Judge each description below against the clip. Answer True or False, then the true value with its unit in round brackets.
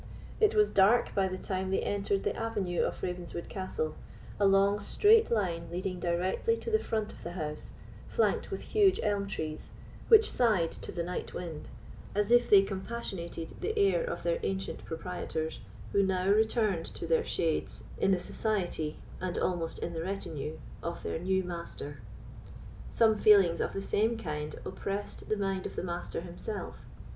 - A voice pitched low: False (190 Hz)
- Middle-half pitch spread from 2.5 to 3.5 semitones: False (3.9 semitones)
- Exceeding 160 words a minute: True (170 wpm)